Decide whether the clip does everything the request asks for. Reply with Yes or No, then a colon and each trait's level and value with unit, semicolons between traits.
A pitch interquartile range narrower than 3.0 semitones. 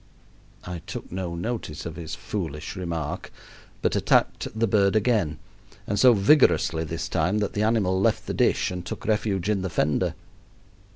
No: average, 4.0 semitones